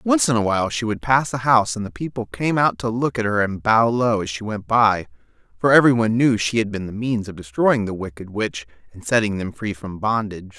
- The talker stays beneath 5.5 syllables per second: No, 5.6 syllables/s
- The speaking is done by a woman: No, male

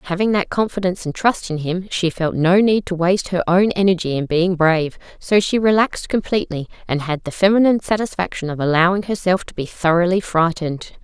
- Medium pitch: Yes, medium, 180 Hz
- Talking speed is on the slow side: No, average, 190 wpm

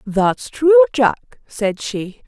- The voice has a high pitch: Yes, high, 235 Hz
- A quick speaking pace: No, slow, 130 wpm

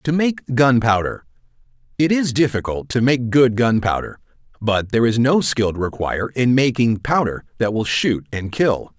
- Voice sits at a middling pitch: No, low, 120 Hz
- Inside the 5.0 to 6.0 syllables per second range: No, 4.6 syllables/s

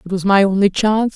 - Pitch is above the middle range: Yes, high, 200 Hz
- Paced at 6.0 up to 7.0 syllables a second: Yes, 6.5 syllables/s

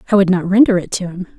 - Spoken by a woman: Yes, female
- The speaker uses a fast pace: Yes, fast, 305 wpm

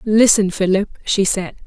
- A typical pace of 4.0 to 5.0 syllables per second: Yes, 4.5 syllables/s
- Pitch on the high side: Yes, high, 200 Hz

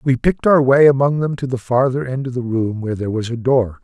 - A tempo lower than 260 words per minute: No, fast, 280 wpm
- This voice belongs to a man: Yes, male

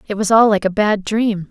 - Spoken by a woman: Yes, female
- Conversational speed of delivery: No, fast, 280 wpm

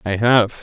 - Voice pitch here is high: No, low, 110 Hz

